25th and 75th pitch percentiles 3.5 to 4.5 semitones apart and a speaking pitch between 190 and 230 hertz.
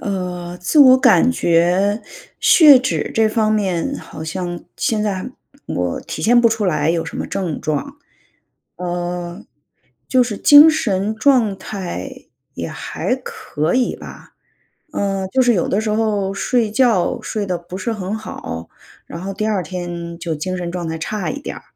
Yes: average, 4.1 semitones; high, 195 Hz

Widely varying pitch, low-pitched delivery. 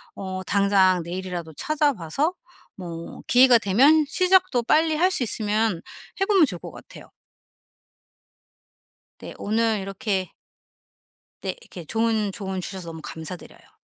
No: wide, 6.3 semitones; high, 205 Hz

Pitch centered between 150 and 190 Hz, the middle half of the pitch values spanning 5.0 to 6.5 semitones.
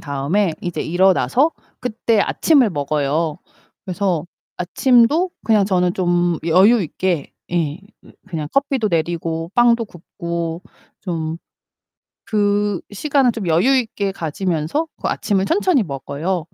Yes: medium, 185 Hz; average, 5.3 semitones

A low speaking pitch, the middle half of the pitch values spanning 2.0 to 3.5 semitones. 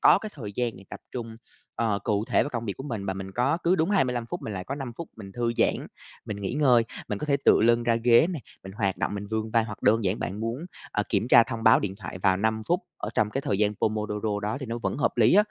Yes: low, 115 Hz; average, 3.2 semitones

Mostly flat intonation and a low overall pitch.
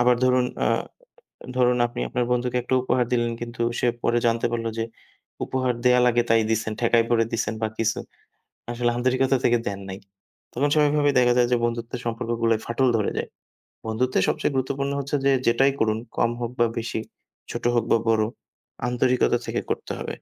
Yes: narrow, 1.7 semitones; low, 120 Hz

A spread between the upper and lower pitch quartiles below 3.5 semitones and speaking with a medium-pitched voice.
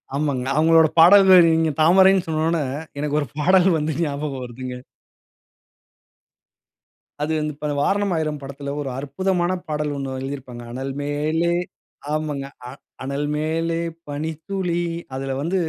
Yes: average, 3.1 semitones; medium, 155 Hz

